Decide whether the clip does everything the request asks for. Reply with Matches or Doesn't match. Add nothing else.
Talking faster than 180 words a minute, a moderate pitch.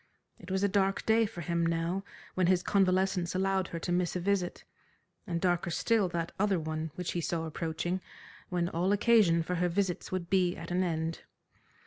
Matches